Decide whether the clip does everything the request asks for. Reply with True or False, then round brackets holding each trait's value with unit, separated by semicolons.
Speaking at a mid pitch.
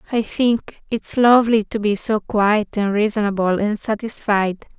False (215 Hz)